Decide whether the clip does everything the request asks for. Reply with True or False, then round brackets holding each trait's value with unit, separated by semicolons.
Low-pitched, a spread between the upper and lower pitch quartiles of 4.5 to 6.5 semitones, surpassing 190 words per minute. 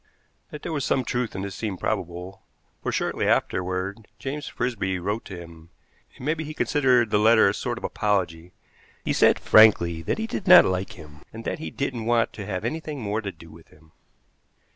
True (105 Hz; 5.3 semitones; 205 wpm)